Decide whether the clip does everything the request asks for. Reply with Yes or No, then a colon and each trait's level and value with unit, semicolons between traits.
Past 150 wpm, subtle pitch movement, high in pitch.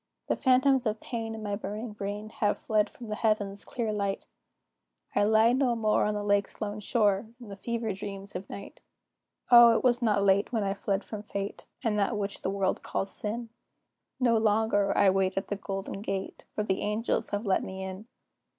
Yes: average, 200 wpm; narrow, 2.1 semitones; high, 210 Hz